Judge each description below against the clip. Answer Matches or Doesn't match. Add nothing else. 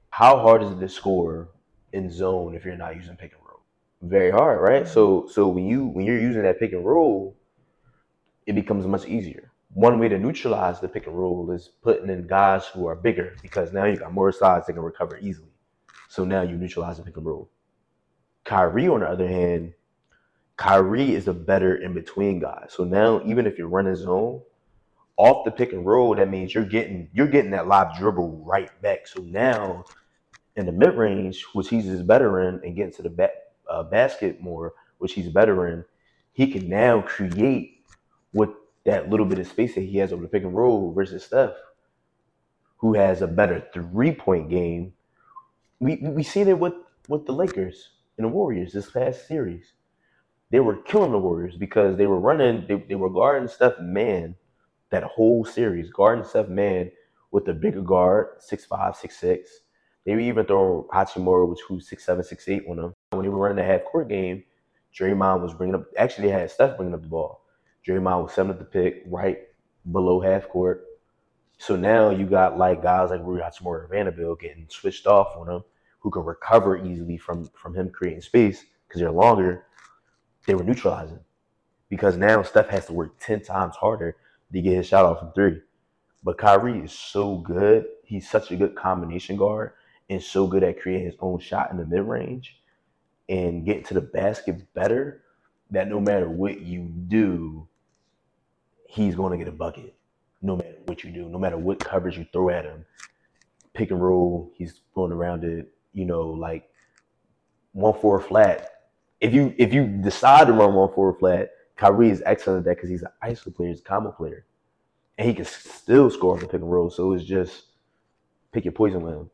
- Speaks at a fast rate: Doesn't match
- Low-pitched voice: Matches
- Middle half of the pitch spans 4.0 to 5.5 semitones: Doesn't match